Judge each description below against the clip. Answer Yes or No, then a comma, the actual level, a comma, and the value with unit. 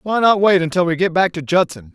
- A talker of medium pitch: Yes, medium, 175 Hz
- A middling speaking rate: No, fast, 280 wpm